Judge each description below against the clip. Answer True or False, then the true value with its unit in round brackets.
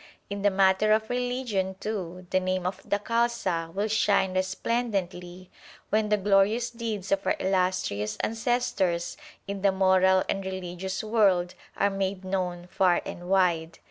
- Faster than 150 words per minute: False (145 wpm)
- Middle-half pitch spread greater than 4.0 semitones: False (2.5 semitones)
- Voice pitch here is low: False (190 Hz)